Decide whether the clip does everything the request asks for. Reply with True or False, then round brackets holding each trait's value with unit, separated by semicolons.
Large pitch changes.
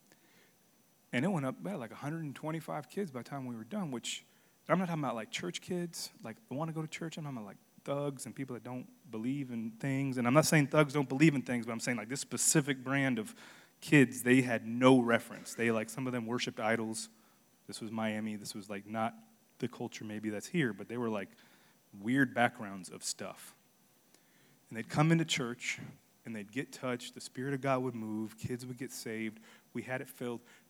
False (4.1 semitones)